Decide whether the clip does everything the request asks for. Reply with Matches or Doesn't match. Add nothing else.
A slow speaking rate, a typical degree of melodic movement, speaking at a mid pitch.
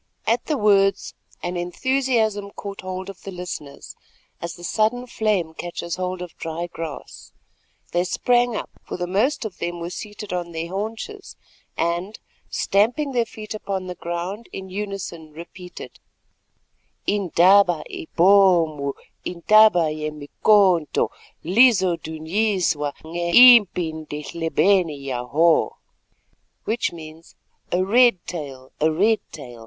Matches